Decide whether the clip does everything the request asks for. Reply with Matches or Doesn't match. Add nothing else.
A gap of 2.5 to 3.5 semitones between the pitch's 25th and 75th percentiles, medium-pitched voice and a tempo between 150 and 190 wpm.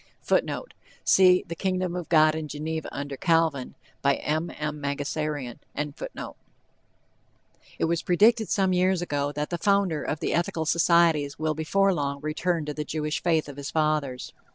Matches